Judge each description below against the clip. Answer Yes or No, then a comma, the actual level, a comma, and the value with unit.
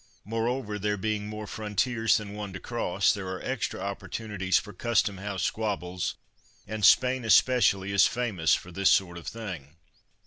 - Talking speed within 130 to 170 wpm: Yes, average, 160 wpm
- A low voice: Yes, low, 105 Hz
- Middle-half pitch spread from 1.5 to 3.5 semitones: Yes, average, 2.8 semitones